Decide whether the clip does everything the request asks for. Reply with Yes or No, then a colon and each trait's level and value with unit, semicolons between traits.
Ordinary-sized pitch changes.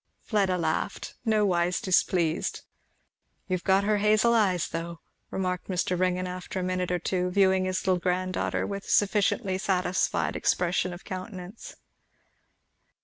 No: narrow, 1.6 semitones